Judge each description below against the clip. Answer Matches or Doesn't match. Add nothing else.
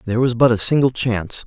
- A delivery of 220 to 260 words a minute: Matches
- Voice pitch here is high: Doesn't match